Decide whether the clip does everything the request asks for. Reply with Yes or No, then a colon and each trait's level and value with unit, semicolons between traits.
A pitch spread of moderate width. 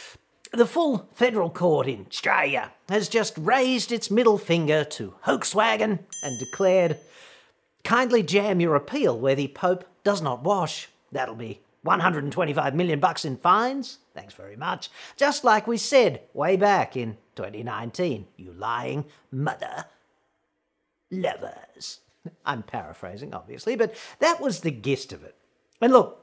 No: wide, 7.5 semitones